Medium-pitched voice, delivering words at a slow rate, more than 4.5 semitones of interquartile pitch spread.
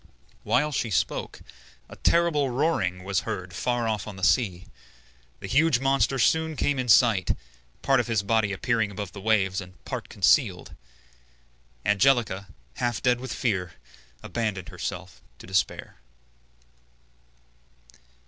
No: low, 110 Hz; slow, 130 wpm; average, 5.3 semitones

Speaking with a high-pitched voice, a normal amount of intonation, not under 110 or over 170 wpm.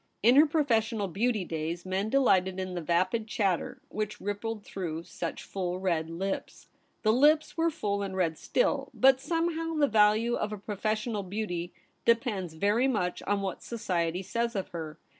Yes: high, 205 Hz; average, 4.4 semitones; average, 165 wpm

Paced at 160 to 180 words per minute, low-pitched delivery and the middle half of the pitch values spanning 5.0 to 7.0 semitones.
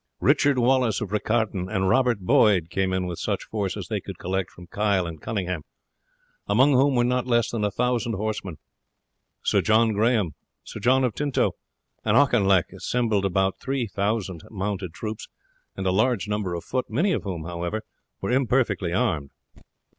No: average, 165 wpm; low, 105 Hz; average, 4.6 semitones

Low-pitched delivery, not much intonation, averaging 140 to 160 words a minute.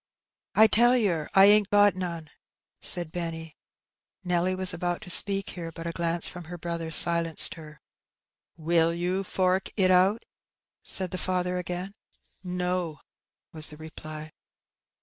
No: medium, 175 Hz; narrow, 2.1 semitones; average, 150 wpm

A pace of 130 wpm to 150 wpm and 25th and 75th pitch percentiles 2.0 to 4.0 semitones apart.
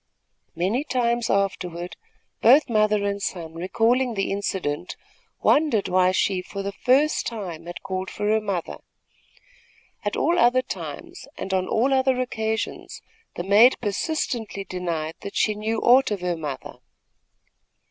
No: average, 140 wpm; average, 4.7 semitones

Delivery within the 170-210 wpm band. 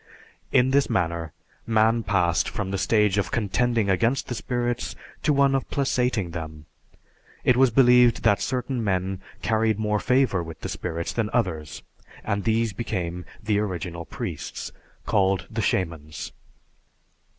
No: average, 140 wpm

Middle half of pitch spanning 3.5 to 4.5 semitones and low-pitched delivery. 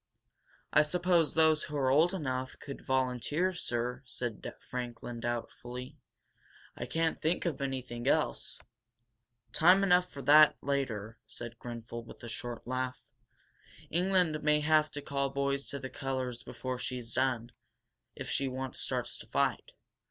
Yes: average, 3.9 semitones; low, 130 Hz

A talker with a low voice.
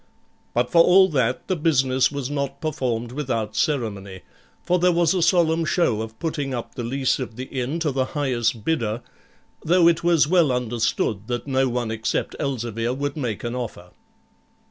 Yes: low, 130 Hz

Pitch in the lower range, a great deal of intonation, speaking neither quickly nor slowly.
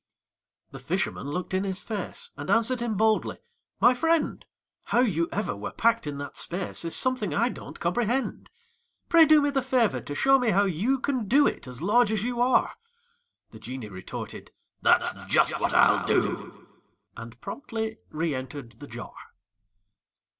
No: high, 215 Hz; wide, 8.1 semitones; average, 165 wpm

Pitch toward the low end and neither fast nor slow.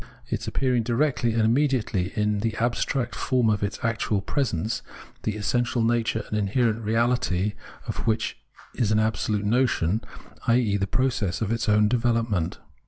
Yes: low, 115 Hz; average, 150 wpm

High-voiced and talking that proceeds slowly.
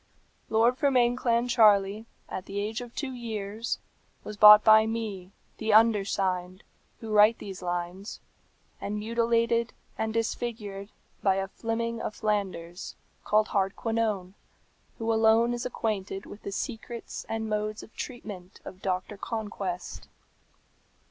Yes: high, 215 Hz; slow, 125 wpm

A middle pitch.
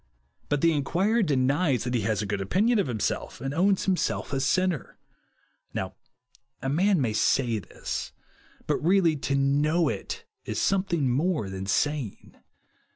Yes: medium, 145 Hz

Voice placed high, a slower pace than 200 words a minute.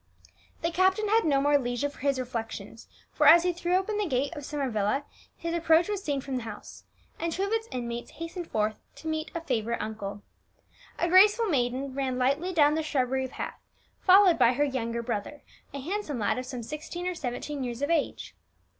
No: very high, 285 Hz; fast, 205 wpm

